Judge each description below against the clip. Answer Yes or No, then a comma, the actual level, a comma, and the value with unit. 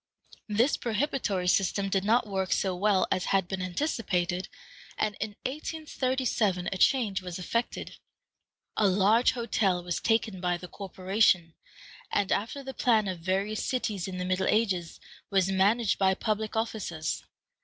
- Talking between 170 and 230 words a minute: No, average, 145 wpm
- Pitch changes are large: No, average, 3.4 semitones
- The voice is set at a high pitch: Yes, high, 195 Hz